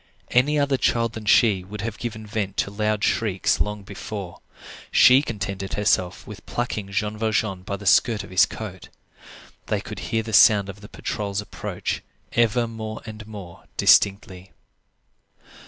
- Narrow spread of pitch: Yes, narrow, 2.1 semitones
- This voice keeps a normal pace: Yes, average, 155 wpm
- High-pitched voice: No, low, 105 Hz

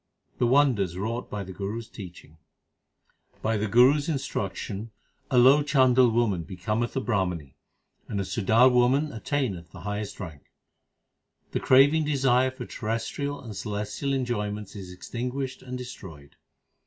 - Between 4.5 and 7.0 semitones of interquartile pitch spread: Yes, average, 4.8 semitones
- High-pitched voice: No, low, 115 Hz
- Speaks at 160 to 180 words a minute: No, average, 150 wpm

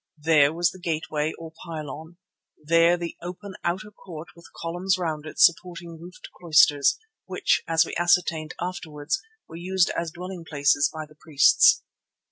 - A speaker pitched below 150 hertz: No, medium, 165 Hz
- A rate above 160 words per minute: No, average, 150 wpm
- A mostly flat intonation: Yes, narrow, 2.3 semitones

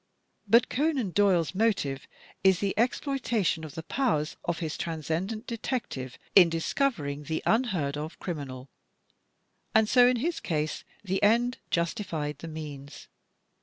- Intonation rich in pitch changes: Yes, wide, 7.0 semitones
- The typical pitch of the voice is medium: Yes, medium, 180 Hz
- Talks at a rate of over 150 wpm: No, slow, 135 wpm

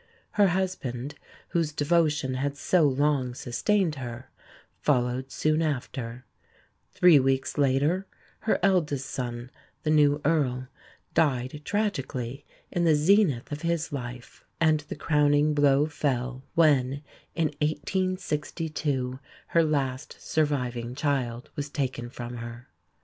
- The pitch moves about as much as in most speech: Yes, average, 3.5 semitones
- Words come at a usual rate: No, slow, 115 wpm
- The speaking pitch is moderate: Yes, medium, 145 Hz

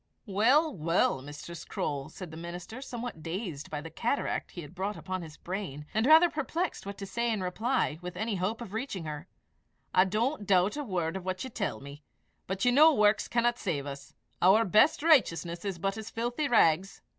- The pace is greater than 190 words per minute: Yes, average, 200 wpm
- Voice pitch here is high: Yes, high, 195 Hz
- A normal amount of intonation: No, wide, 5.7 semitones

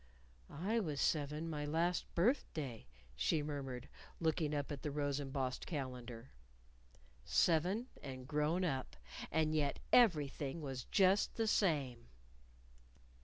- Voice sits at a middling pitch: Yes, medium, 150 Hz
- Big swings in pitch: No, average, 3.7 semitones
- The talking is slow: Yes, slow, 120 wpm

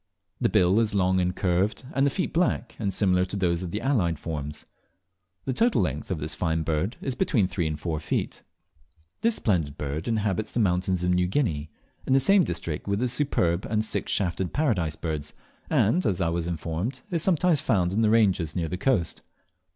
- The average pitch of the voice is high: No, very low, 95 Hz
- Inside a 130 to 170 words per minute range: No, average, 200 wpm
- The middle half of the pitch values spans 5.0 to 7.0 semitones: Yes, wide, 5.6 semitones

